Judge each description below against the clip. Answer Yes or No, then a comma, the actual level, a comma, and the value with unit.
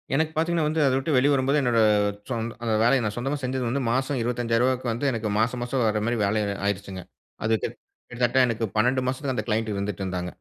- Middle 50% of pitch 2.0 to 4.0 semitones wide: Yes, average, 3.0 semitones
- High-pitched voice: No, low, 120 Hz